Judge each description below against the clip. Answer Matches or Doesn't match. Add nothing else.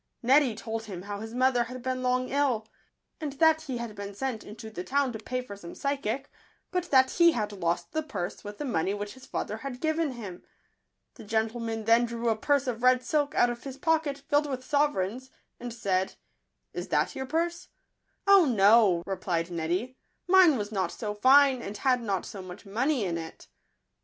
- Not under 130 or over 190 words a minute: Doesn't match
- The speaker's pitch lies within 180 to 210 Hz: Doesn't match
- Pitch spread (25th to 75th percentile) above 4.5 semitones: Matches